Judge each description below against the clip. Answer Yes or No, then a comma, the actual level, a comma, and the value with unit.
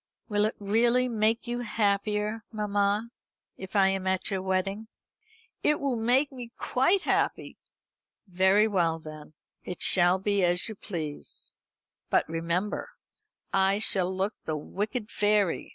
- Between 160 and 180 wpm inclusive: No, average, 140 wpm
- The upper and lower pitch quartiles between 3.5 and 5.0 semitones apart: No, average, 2.9 semitones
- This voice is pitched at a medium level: No, high, 205 Hz